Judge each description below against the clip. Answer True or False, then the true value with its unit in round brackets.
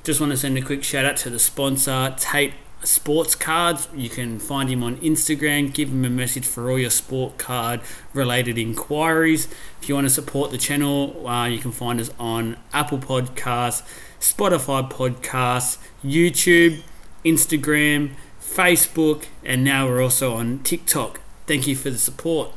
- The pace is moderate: True (165 wpm)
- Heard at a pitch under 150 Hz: True (135 Hz)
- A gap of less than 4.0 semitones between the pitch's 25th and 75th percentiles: True (3.3 semitones)